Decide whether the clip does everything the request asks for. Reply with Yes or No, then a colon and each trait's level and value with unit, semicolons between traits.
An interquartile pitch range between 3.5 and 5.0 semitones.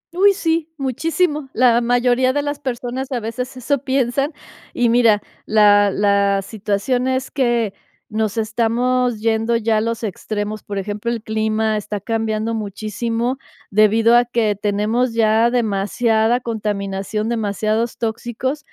No: narrow, 2.6 semitones